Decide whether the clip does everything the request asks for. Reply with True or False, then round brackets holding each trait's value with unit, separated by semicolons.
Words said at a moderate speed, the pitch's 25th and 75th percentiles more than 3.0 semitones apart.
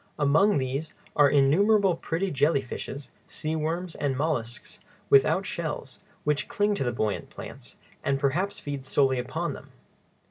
True (145 wpm; 4.0 semitones)